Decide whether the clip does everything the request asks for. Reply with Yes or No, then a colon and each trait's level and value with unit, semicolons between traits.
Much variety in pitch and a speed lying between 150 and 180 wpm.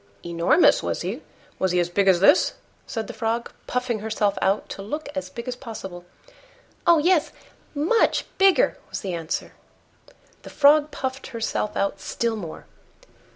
Yes: wide, 6.8 semitones; average, 155 wpm